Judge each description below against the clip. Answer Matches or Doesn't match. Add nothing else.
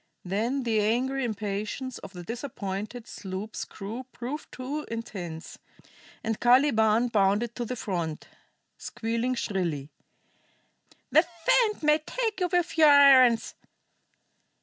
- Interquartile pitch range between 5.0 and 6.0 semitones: Doesn't match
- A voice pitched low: Doesn't match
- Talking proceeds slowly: Matches